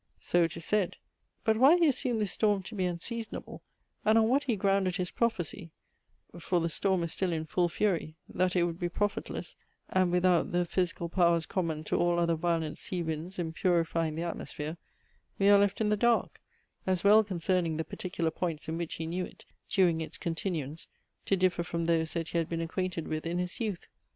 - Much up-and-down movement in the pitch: No, average, 2.9 semitones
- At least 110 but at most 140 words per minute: No, fast, 205 wpm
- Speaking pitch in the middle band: Yes, medium, 175 Hz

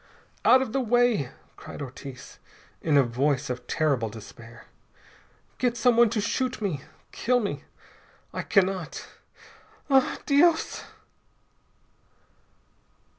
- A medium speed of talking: No, slow, 105 wpm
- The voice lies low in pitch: No, high, 195 Hz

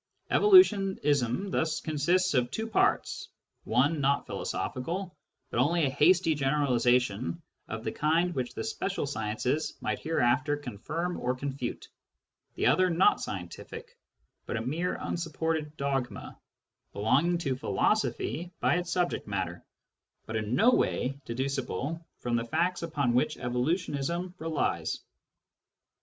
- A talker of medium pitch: Yes, medium, 145 Hz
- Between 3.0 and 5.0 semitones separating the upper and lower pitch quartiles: No, wide, 5.5 semitones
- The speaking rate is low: Yes, slow, 125 wpm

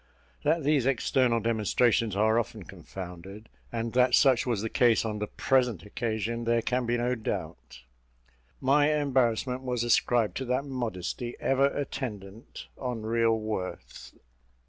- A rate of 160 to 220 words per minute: No, average, 140 wpm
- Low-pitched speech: Yes, low, 115 Hz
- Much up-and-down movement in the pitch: No, average, 2.9 semitones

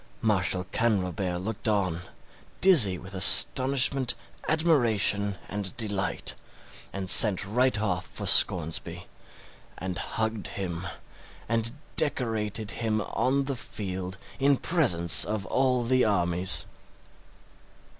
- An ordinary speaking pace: No, slow, 105 wpm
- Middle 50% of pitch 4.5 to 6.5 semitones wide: Yes, average, 4.8 semitones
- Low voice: Yes, low, 105 Hz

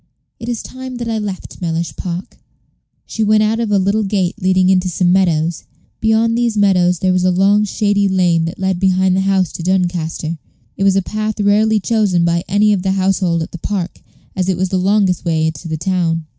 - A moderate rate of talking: No, fast, 210 wpm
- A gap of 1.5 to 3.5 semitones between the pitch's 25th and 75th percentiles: Yes, average, 2.9 semitones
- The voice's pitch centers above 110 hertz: Yes, high, 190 Hz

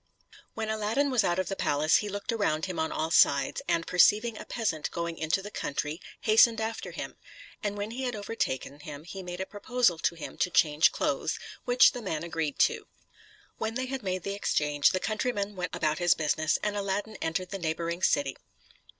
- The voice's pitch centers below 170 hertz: No, medium, 185 Hz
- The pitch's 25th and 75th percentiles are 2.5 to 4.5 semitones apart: No, average, 5.2 semitones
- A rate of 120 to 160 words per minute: No, average, 195 wpm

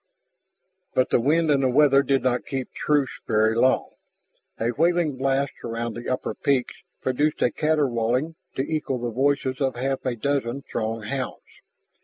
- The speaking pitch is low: Yes, low, 130 Hz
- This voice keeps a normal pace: Yes, average, 160 wpm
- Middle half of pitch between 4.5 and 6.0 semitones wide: No, average, 2.8 semitones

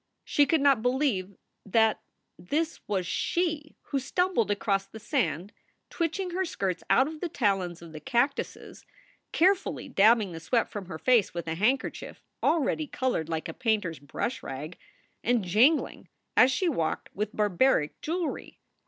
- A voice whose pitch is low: No, high, 225 Hz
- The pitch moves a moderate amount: No, wide, 7.8 semitones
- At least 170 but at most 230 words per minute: No, average, 160 wpm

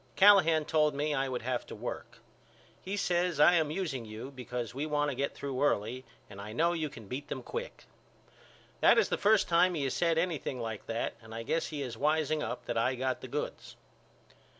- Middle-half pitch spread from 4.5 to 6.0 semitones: Yes, average, 4.8 semitones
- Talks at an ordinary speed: No, fast, 215 wpm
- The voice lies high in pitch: No, medium, 145 Hz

